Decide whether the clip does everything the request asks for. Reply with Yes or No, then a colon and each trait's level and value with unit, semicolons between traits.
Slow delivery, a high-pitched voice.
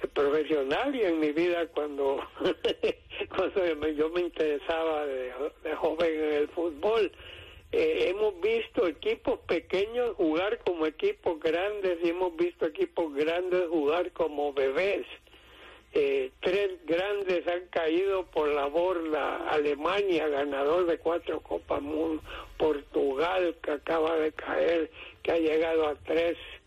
No: slow, 125 wpm; medium, 170 Hz